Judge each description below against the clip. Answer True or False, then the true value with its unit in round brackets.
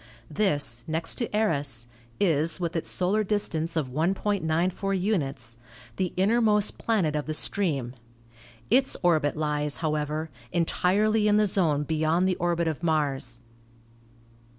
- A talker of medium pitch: True (165 Hz)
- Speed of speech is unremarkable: False (130 wpm)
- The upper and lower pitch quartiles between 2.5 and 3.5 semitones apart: False (4.7 semitones)